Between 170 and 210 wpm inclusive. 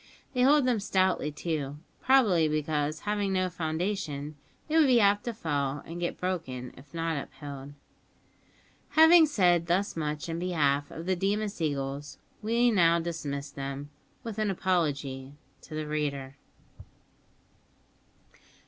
No: slow, 135 wpm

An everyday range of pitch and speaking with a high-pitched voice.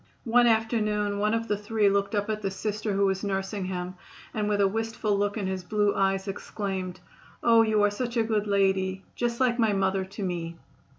No: narrow, 2.2 semitones; high, 205 Hz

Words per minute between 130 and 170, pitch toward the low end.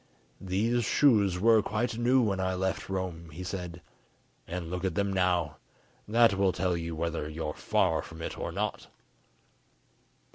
Yes: average, 160 wpm; very low, 95 Hz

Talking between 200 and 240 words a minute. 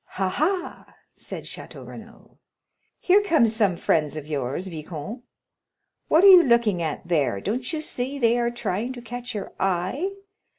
No: average, 160 wpm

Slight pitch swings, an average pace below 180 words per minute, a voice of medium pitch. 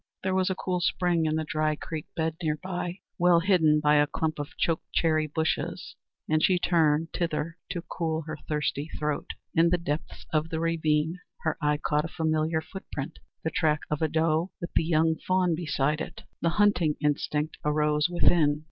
No: narrow, 2.1 semitones; average, 185 wpm; medium, 160 Hz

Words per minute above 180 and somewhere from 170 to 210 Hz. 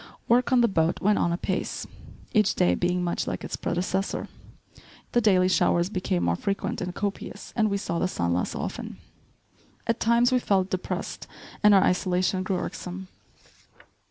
No: average, 165 wpm; medium, 185 Hz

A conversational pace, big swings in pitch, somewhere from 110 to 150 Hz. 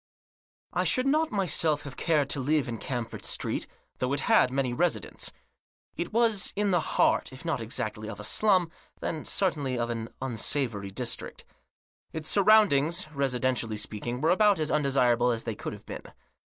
Yes: average, 170 wpm; wide, 6.3 semitones; medium, 140 Hz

